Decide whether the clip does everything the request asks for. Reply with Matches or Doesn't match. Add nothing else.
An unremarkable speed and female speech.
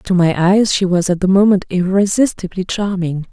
Matches